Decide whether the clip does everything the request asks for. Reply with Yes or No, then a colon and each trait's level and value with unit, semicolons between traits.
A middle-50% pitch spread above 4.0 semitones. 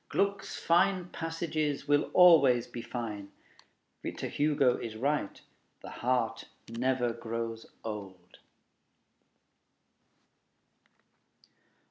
Yes: average, 5.2 semitones